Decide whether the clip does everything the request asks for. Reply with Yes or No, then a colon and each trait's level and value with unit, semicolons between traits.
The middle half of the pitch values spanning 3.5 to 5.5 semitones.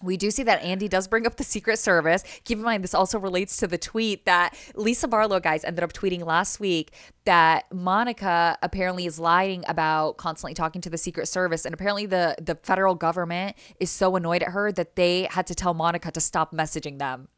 No: average, 2.8 semitones